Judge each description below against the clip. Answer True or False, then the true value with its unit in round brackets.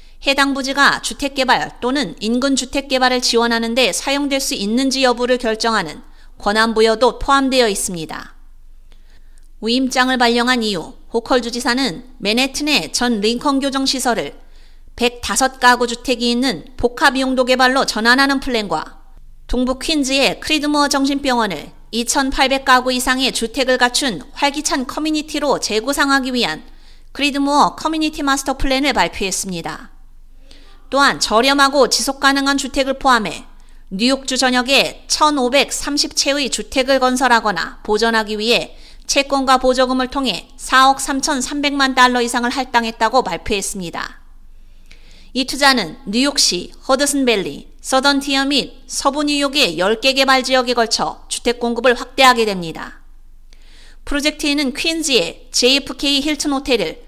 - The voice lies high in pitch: True (260 Hz)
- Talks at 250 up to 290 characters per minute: False (300 characters per minute)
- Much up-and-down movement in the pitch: False (2.6 semitones)